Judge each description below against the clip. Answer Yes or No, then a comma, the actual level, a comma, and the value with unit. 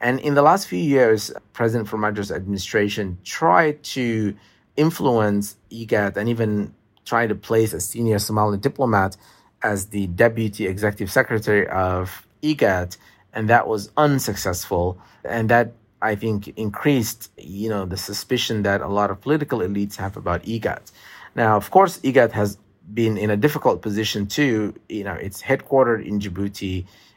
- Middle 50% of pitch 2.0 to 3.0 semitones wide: Yes, narrow, 2.6 semitones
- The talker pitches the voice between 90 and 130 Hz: Yes, low, 105 Hz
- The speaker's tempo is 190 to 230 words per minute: No, average, 150 wpm